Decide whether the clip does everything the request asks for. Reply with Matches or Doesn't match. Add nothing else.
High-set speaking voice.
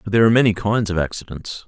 Doesn't match